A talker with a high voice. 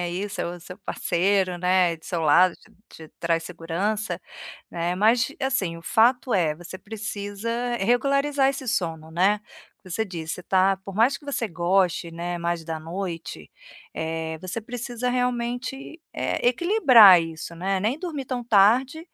Yes: high, 195 Hz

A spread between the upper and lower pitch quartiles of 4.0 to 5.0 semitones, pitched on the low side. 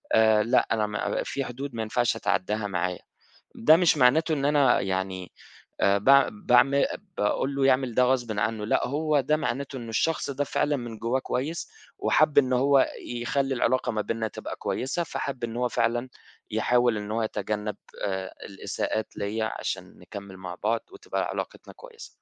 Yes: average, 4.5 semitones; low, 120 Hz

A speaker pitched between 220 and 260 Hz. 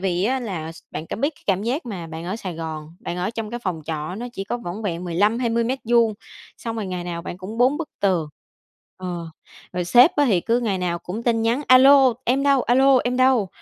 No: high, 210 Hz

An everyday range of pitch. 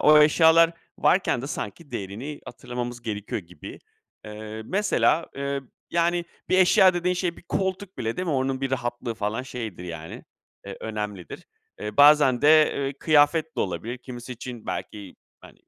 No: wide, 6.6 semitones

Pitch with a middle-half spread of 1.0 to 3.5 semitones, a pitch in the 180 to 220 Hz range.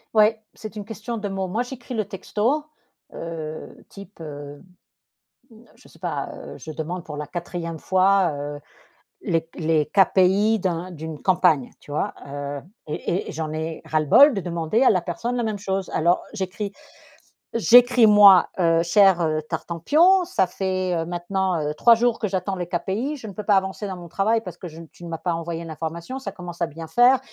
No: average, 4.4 semitones; medium, 185 Hz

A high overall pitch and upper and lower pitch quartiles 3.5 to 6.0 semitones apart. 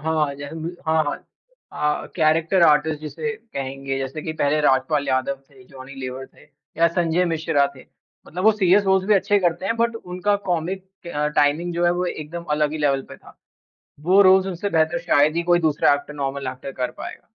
No: medium, 160 Hz; average, 4.0 semitones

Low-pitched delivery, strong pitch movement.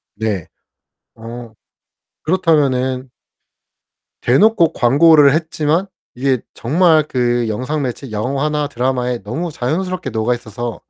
No: low, 130 Hz; average, 4.5 semitones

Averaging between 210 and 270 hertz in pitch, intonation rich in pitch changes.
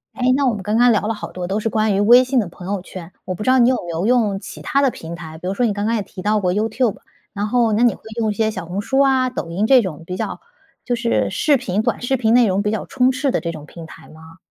No: high, 215 Hz; average, 5.0 semitones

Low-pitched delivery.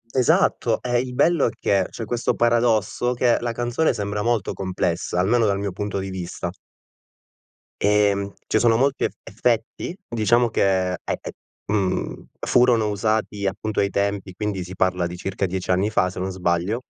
Yes: low, 105 Hz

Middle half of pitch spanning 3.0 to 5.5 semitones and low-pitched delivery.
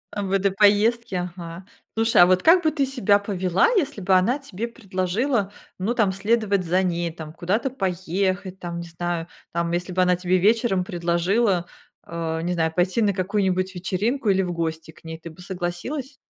No: average, 3.4 semitones; medium, 185 Hz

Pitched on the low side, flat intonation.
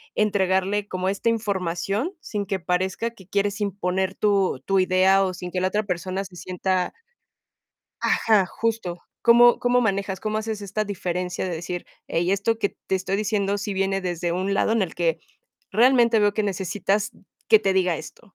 No: high, 195 Hz; narrow, 2.3 semitones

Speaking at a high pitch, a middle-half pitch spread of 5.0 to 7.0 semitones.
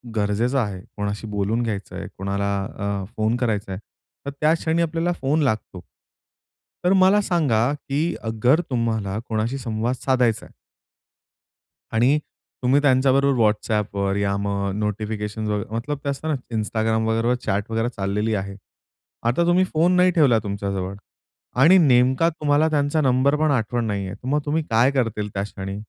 No: low, 115 Hz; wide, 5.5 semitones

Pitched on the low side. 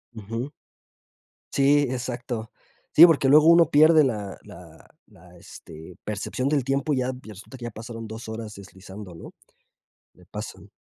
Yes: low, 120 Hz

